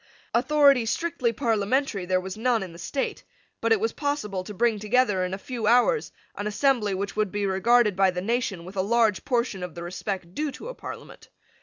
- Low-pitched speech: No, high, 215 Hz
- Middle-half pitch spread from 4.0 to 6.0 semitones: Yes, average, 4.8 semitones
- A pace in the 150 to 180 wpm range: No, fast, 205 wpm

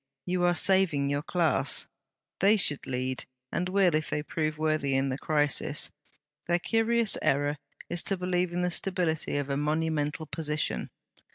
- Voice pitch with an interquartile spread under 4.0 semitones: Yes, average, 3.5 semitones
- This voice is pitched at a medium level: Yes, medium, 160 Hz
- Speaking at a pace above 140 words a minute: Yes, average, 160 wpm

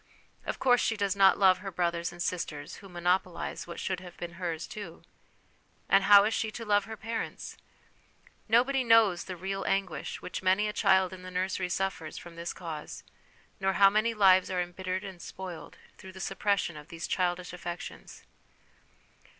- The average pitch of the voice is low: No, medium, 185 Hz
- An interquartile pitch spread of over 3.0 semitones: No, narrow, 2.4 semitones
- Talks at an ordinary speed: Yes, average, 175 wpm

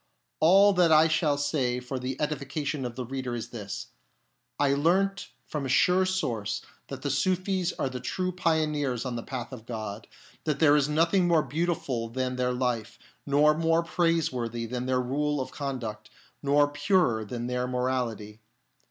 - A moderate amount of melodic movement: Yes, average, 4.4 semitones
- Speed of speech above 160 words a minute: Yes, average, 170 wpm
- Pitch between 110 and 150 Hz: Yes, low, 135 Hz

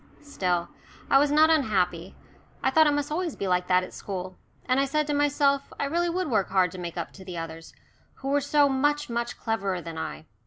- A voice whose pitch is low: No, very high, 255 Hz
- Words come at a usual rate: No, fast, 225 wpm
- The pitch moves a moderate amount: No, wide, 8.1 semitones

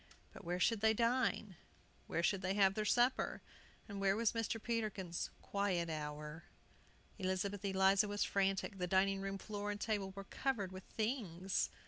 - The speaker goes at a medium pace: Yes, average, 160 wpm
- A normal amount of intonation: No, narrow, 2.3 semitones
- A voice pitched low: No, high, 195 Hz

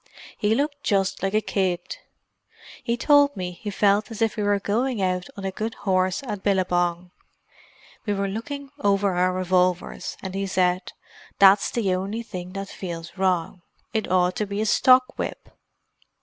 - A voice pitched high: Yes, high, 195 Hz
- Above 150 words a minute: Yes, average, 170 wpm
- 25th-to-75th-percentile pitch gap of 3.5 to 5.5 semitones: No, average, 2.8 semitones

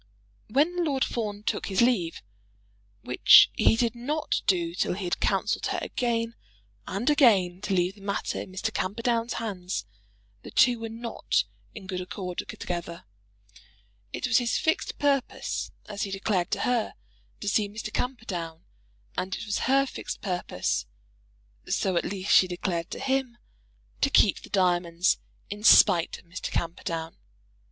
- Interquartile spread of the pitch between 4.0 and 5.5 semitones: Yes, average, 4.8 semitones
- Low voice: No, high, 205 Hz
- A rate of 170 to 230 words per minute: No, average, 155 wpm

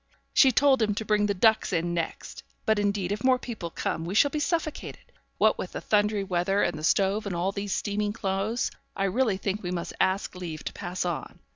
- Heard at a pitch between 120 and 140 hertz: No, high, 200 Hz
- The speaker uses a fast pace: Yes, fast, 220 wpm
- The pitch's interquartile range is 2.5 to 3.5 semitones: Yes, average, 3.1 semitones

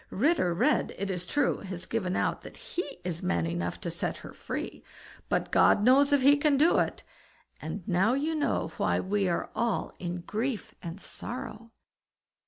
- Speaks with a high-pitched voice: Yes, high, 210 Hz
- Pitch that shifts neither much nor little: No, wide, 7.7 semitones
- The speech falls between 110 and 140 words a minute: No, average, 180 wpm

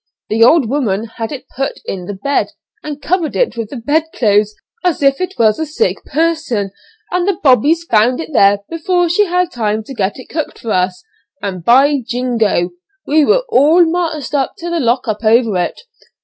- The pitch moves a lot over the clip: Yes, wide, 7.1 semitones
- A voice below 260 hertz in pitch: No, very high, 270 Hz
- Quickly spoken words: No, average, 195 wpm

